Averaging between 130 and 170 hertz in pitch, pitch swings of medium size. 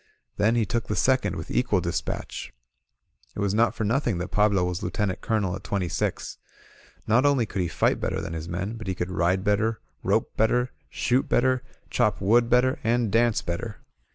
No: low, 105 Hz; average, 4.0 semitones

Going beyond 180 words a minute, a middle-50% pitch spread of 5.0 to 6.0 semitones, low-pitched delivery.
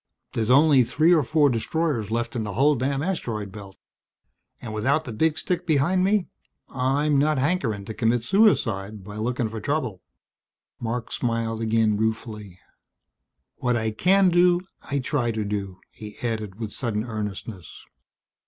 No: average, 155 wpm; wide, 5.4 semitones; low, 120 Hz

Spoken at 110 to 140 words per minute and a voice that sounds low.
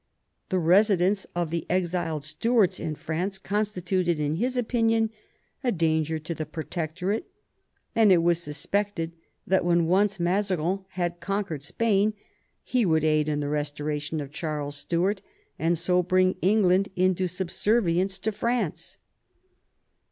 No: slow, 135 wpm; medium, 180 Hz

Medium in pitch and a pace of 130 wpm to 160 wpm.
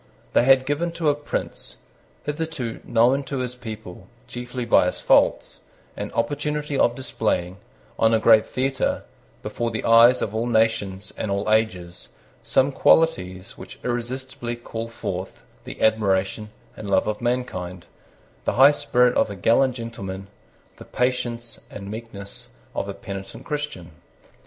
No: low, 115 Hz; average, 145 wpm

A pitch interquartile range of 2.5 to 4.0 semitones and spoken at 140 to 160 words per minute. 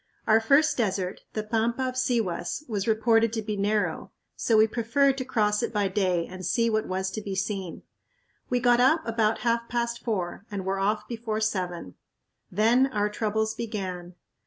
No: average, 3.0 semitones; average, 180 wpm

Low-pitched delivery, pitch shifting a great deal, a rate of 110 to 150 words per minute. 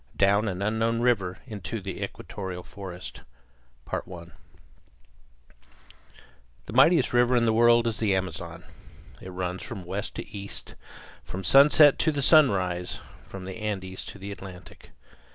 No: low, 100 Hz; average, 4.2 semitones; slow, 135 wpm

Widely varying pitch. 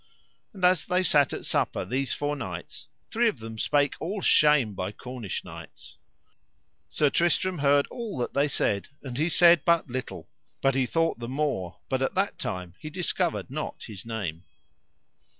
Yes: wide, 6.2 semitones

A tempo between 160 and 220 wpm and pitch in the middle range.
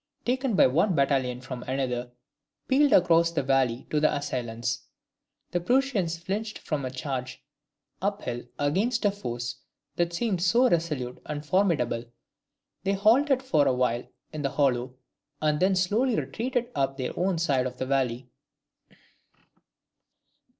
No: average, 145 wpm; medium, 150 Hz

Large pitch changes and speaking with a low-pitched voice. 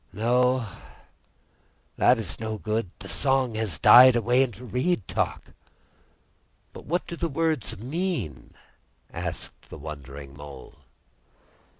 Yes: wide, 6.4 semitones; low, 115 Hz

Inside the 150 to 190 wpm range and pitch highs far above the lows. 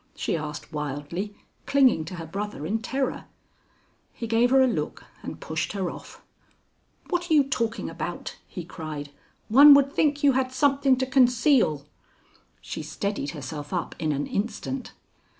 Yes: average, 155 wpm; wide, 9.0 semitones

